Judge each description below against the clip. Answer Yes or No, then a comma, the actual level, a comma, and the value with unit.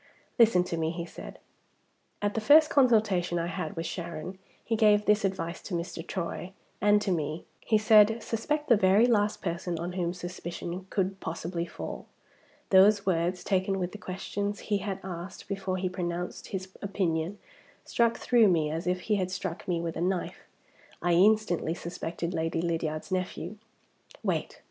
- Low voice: No, medium, 185 Hz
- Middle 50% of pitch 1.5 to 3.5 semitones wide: Yes, average, 3.2 semitones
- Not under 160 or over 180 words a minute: Yes, average, 170 wpm